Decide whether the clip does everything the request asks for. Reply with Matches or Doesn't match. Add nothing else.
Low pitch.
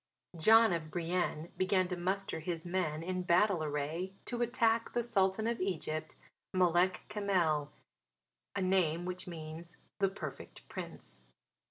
Doesn't match